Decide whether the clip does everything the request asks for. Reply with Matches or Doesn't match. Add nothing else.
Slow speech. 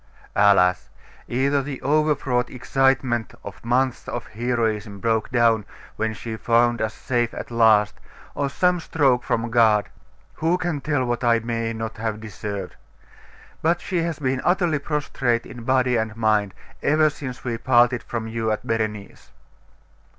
Doesn't match